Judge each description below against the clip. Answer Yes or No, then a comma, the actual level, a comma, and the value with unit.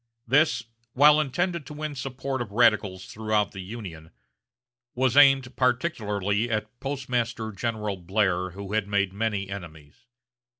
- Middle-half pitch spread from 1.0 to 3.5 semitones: No, average, 4.7 semitones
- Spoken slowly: Yes, slow, 130 wpm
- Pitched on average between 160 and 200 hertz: No, low, 110 Hz